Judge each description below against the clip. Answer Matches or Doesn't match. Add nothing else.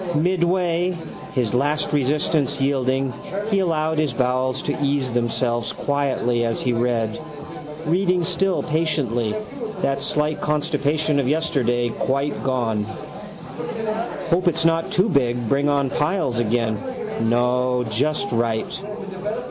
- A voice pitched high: Doesn't match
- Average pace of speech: Doesn't match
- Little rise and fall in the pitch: Doesn't match